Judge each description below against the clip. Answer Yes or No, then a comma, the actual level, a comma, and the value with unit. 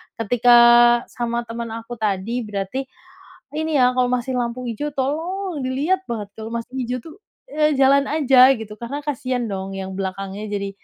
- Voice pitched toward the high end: Yes, high, 245 Hz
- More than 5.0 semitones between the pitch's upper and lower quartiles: No, average, 3.7 semitones